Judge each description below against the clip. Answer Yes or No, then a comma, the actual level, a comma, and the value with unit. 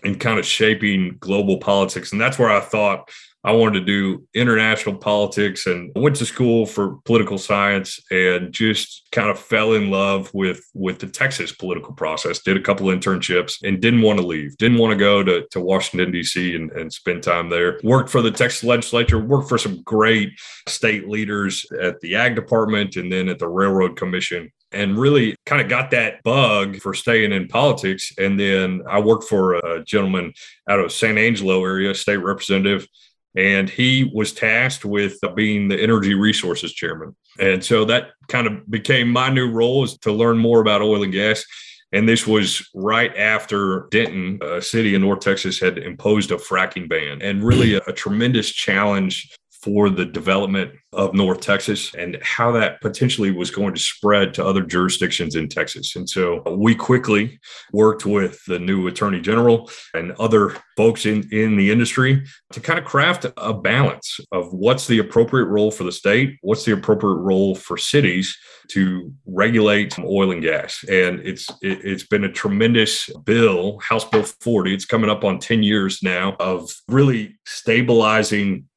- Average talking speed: Yes, average, 180 wpm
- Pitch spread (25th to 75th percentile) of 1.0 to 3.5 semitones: Yes, average, 2.9 semitones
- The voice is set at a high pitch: No, low, 100 Hz